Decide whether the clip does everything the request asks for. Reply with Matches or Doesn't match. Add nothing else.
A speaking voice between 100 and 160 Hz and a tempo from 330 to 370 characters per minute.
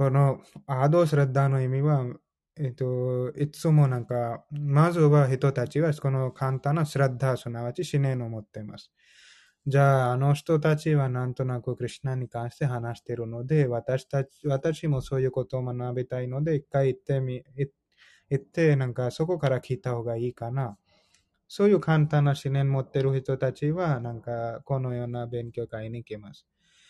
Matches